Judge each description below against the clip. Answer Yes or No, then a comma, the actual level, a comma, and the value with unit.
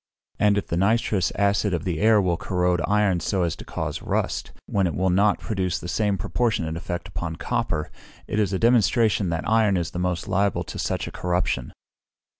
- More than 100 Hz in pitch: No, very low, 95 Hz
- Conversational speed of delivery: Yes, average, 195 wpm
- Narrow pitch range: No, average, 3.2 semitones